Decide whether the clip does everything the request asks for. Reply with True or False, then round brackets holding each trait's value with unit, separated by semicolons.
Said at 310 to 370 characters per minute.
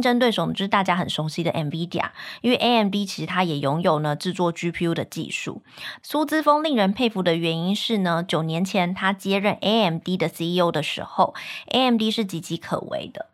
True (340 characters per minute)